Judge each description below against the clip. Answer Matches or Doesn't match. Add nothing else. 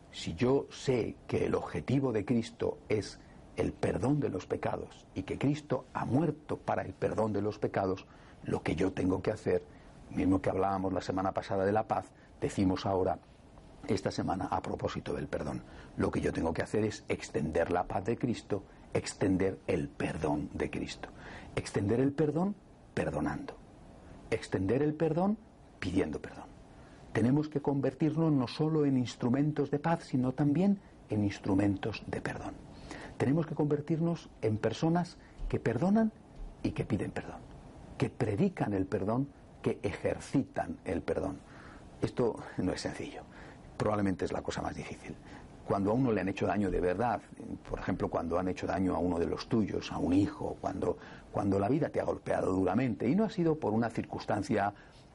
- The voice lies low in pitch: Matches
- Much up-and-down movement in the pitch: Matches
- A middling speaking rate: Matches